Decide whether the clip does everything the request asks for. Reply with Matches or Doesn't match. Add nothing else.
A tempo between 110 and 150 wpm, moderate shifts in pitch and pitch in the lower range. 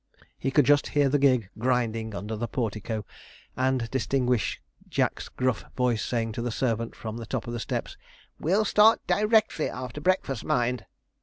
Doesn't match